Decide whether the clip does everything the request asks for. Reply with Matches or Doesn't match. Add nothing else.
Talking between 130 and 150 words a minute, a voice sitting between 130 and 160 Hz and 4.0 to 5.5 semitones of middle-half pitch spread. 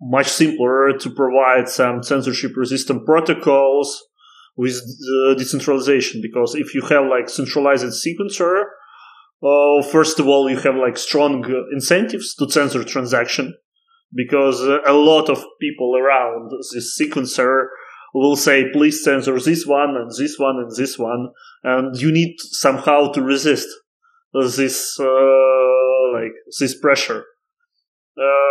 Doesn't match